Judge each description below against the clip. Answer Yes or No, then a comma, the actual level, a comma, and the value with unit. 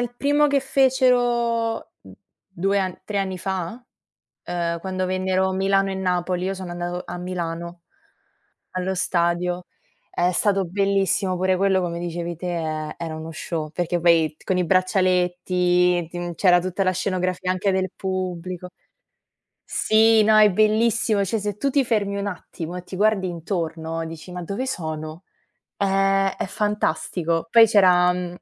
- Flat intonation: Yes, narrow, 2.3 semitones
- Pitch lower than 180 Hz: No, medium, 185 Hz